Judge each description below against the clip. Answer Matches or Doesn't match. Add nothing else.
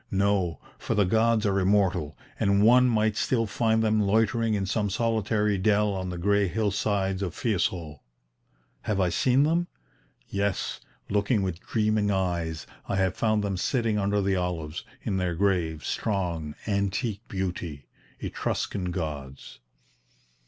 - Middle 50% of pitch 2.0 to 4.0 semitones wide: Matches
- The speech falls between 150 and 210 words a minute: Doesn't match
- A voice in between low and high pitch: Doesn't match